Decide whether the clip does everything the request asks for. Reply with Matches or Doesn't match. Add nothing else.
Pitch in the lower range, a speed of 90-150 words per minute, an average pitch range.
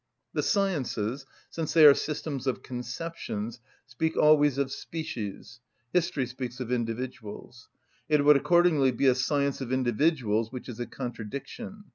Matches